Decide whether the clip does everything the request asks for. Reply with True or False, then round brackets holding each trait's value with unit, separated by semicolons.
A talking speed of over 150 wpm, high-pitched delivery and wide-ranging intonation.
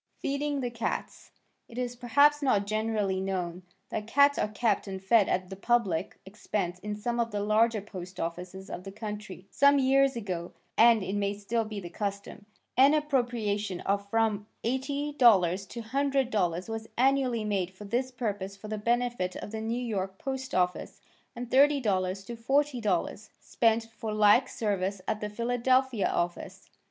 False (165 wpm; 215 Hz; 3.9 semitones)